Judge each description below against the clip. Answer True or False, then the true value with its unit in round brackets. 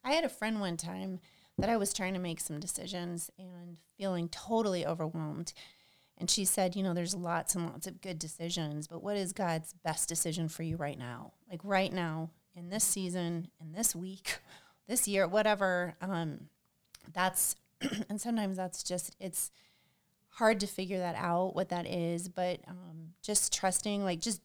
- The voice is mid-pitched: True (180 Hz)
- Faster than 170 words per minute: True (180 wpm)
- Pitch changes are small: True (2.3 semitones)